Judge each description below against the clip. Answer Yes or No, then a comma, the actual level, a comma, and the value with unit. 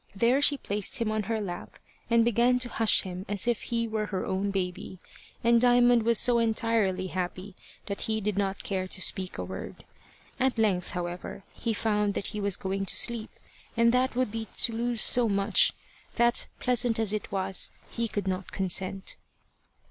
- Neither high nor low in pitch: No, high, 215 Hz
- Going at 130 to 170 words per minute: No, average, 185 wpm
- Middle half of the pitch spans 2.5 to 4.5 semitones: Yes, average, 3.4 semitones